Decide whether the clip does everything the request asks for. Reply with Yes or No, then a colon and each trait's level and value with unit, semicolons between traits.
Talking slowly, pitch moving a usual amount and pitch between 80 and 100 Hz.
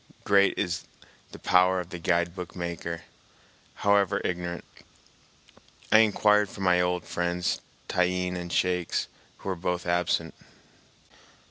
No: slow, 120 wpm; narrow, 1.4 semitones; very low, 90 Hz